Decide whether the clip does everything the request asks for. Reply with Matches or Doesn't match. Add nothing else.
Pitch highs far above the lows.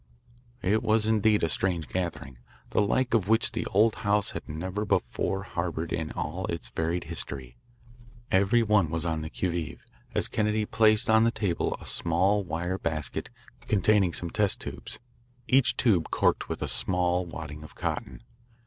Doesn't match